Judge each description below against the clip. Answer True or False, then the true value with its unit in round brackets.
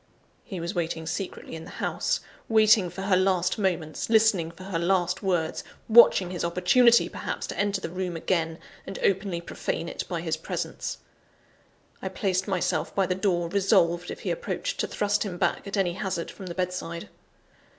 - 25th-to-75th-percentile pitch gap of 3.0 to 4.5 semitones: False (2.5 semitones)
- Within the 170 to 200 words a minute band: True (180 wpm)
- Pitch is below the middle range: False (185 Hz)